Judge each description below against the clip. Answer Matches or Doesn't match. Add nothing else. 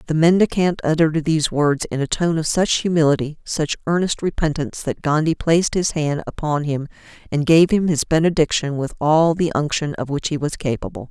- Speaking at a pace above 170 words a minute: Matches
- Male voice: Doesn't match